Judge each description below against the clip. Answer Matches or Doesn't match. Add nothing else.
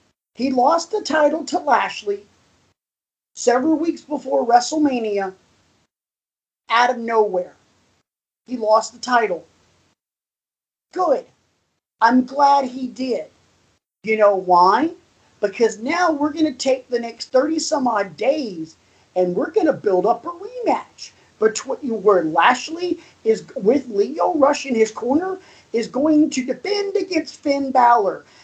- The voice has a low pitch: Doesn't match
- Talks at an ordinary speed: Doesn't match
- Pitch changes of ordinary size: Doesn't match